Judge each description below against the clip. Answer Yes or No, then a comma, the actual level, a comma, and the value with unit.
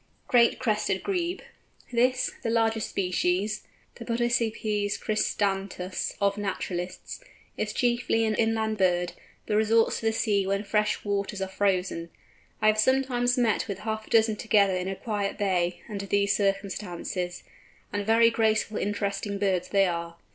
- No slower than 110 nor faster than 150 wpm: Yes, average, 145 wpm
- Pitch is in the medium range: No, high, 205 Hz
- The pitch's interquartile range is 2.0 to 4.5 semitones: Yes, narrow, 2.5 semitones